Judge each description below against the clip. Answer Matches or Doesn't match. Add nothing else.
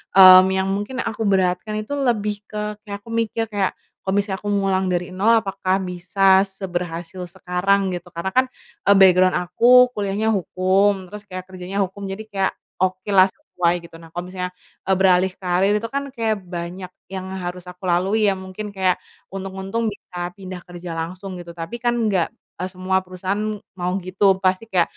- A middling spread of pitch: Doesn't match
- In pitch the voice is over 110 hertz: Matches